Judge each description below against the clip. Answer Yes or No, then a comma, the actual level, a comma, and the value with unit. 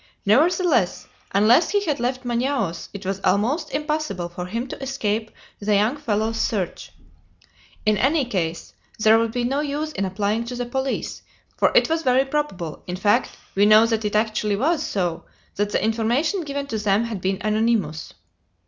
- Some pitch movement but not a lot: Yes, average, 4.9 semitones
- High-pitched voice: Yes, high, 225 Hz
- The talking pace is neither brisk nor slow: Yes, average, 175 wpm